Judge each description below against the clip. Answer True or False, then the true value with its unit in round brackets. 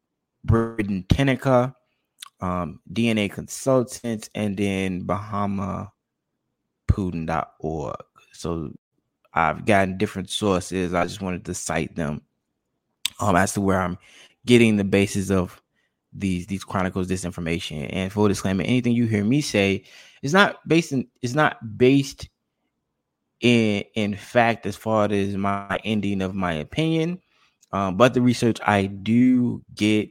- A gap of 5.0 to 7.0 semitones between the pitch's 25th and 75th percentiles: False (4.2 semitones)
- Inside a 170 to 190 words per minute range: False (135 wpm)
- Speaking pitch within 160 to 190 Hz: False (100 Hz)